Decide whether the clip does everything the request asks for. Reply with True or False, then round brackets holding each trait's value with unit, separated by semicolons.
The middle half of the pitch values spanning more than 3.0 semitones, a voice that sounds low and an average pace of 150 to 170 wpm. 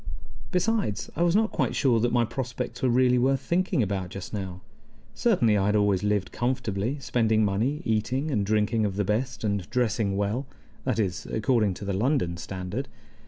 False (4.2 semitones; 110 Hz; 180 wpm)